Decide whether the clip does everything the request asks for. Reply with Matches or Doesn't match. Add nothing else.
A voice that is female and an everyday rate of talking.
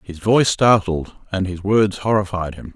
Doesn't match